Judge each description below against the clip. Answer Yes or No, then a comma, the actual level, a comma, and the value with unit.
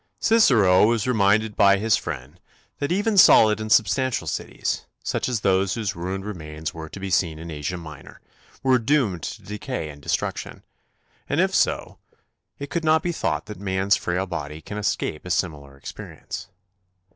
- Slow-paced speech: No, average, 170 wpm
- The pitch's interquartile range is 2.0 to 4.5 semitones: No, average, 5.3 semitones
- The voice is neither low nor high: No, very low, 95 Hz